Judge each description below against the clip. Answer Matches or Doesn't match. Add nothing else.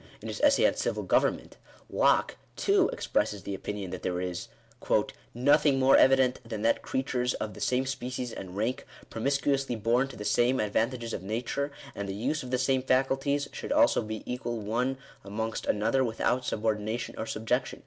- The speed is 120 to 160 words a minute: Doesn't match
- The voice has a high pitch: Doesn't match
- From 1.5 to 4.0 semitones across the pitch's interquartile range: Matches